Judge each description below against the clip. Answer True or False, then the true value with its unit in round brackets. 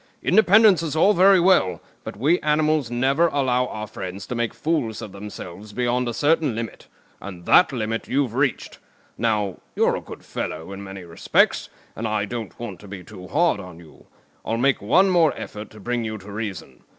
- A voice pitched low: True (115 Hz)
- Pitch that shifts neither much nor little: False (6.6 semitones)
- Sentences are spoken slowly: False (190 wpm)